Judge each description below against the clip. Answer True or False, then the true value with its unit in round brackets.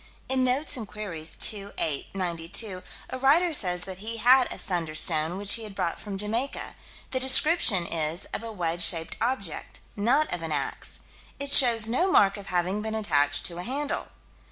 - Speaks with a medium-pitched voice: False (205 Hz)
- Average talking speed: True (180 wpm)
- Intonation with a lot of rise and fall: True (6.3 semitones)